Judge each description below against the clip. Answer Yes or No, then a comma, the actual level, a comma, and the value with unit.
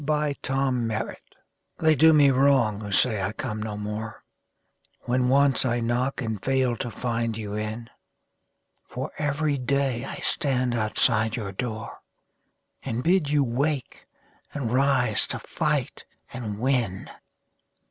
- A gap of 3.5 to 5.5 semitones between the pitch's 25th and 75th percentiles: Yes, average, 3.8 semitones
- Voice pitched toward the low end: Yes, low, 125 Hz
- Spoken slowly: Yes, slow, 130 wpm